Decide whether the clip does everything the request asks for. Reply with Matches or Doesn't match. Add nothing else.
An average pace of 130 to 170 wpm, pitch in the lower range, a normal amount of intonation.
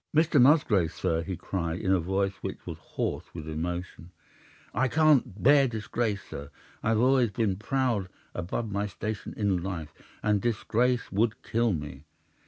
Matches